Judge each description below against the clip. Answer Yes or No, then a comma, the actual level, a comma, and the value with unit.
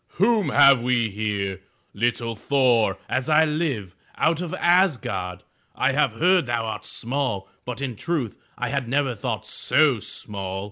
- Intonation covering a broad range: Yes, wide, 5.9 semitones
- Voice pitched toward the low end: Yes, low, 125 Hz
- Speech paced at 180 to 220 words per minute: No, average, 150 wpm